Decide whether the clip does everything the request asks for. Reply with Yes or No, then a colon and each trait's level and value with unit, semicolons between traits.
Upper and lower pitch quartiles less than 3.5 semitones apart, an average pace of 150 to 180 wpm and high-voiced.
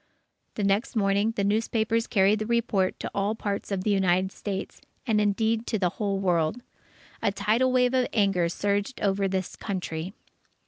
Yes: narrow, 2.4 semitones; average, 170 wpm; high, 205 Hz